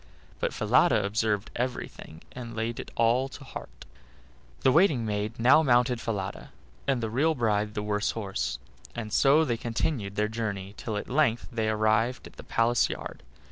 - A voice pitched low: Yes, low, 115 Hz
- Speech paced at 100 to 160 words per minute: No, average, 170 wpm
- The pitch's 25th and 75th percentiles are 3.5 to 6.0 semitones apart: No, average, 2.8 semitones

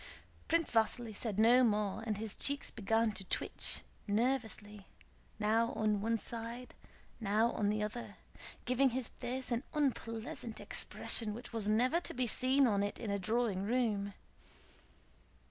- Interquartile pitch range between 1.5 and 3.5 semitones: Yes, narrow, 2.6 semitones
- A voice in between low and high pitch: No, high, 225 Hz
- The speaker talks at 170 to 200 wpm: No, average, 145 wpm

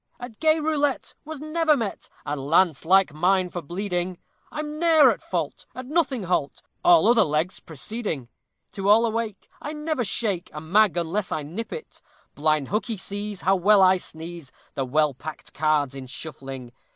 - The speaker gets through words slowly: No, average, 170 wpm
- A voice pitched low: No, high, 190 Hz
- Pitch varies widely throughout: Yes, wide, 7.6 semitones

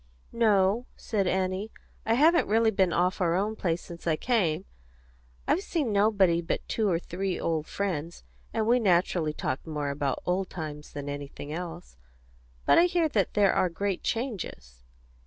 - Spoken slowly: No, average, 165 wpm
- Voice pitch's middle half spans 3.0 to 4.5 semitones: No, average, 4.9 semitones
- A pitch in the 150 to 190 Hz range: Yes, medium, 185 Hz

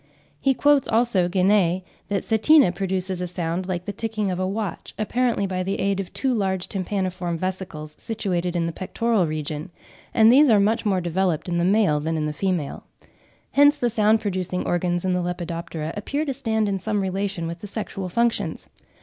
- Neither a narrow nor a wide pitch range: Yes, average, 3.5 semitones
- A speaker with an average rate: Yes, average, 190 wpm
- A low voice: No, high, 190 Hz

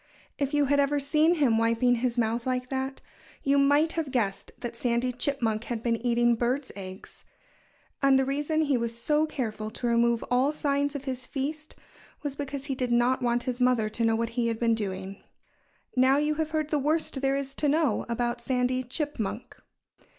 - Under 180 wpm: No, average, 195 wpm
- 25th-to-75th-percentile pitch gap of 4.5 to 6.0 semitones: No, average, 3.3 semitones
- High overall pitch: Yes, very high, 255 Hz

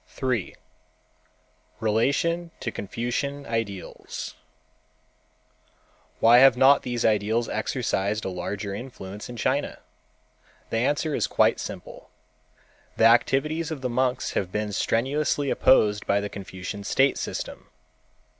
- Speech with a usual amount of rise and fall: Yes, average, 4.6 semitones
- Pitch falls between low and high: No, low, 115 Hz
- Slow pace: Yes, slow, 115 wpm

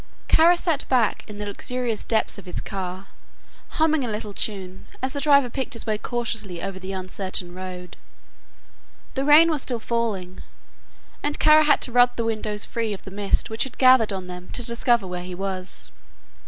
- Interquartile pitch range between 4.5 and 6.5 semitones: Yes, average, 5.0 semitones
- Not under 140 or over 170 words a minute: No, average, 185 wpm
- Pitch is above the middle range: Yes, high, 220 Hz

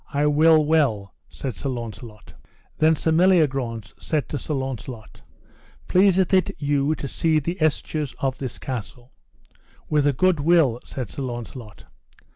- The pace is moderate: Yes, average, 145 wpm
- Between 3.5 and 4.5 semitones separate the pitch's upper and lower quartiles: Yes, average, 4.0 semitones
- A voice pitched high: No, medium, 140 Hz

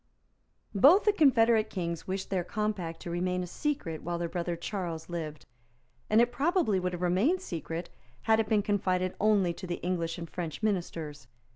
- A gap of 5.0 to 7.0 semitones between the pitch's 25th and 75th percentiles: No, average, 4.1 semitones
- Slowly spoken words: No, average, 175 wpm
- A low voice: No, medium, 185 Hz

